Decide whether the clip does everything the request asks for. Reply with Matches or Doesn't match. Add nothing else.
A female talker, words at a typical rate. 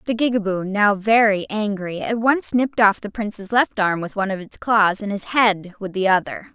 Doesn't match